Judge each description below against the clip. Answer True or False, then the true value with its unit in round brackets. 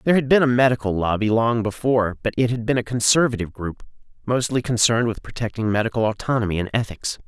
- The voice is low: True (115 Hz)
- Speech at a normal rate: True (190 wpm)